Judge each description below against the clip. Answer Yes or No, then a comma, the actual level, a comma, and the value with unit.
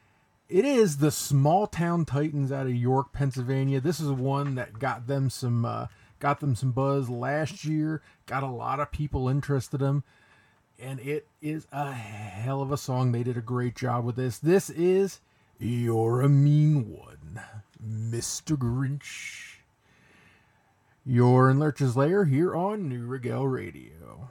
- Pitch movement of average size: Yes, average, 3.1 semitones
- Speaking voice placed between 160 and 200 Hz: No, low, 135 Hz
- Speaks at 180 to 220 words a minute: No, average, 160 wpm